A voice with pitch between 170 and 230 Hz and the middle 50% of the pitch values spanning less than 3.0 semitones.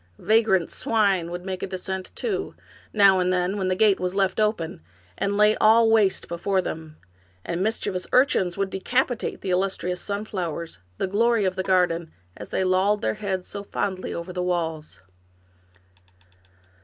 Yes: high, 190 Hz; narrow, 2.5 semitones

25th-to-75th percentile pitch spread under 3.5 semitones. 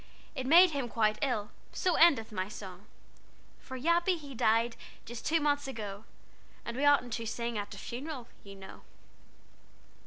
No: average, 5.2 semitones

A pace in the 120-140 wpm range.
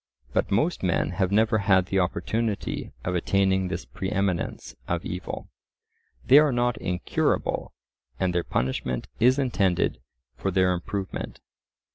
Yes: slow, 135 wpm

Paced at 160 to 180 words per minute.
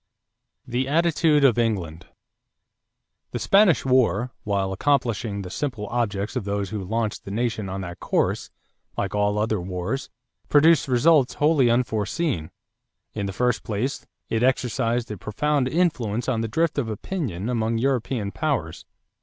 No: average, 145 wpm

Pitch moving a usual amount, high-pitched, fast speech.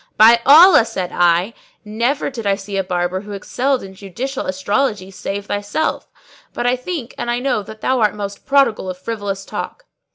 No: average, 4.4 semitones; high, 210 Hz; average, 185 wpm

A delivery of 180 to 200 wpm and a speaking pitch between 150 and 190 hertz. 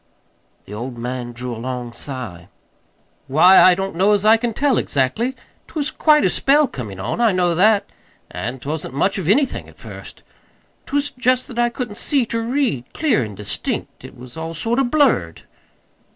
Yes: average, 190 wpm; medium, 185 Hz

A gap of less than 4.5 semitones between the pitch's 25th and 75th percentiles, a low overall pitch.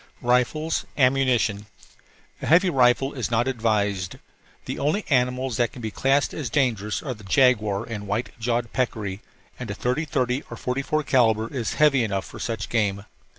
Yes: average, 3.6 semitones; low, 125 Hz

